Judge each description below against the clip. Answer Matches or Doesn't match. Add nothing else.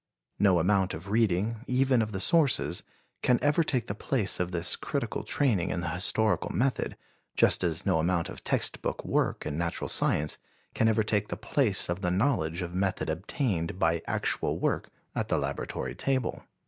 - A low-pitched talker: Matches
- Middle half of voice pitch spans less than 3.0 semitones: Doesn't match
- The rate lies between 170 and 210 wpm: Matches